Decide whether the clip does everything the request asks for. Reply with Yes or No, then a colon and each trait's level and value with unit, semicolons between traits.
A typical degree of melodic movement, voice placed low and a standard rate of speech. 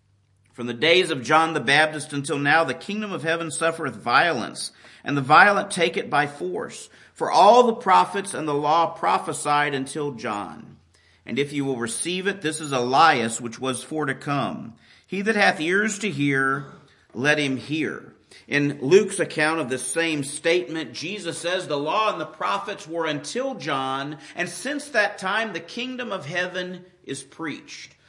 No: average, 4.6 semitones; medium, 155 Hz; average, 175 wpm